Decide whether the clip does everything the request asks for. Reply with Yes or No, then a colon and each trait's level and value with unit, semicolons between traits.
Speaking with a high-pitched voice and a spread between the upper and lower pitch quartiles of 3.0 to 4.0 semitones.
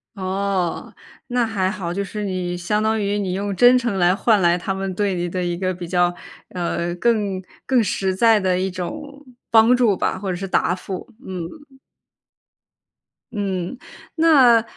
Yes: high, 195 Hz; average, 3.5 semitones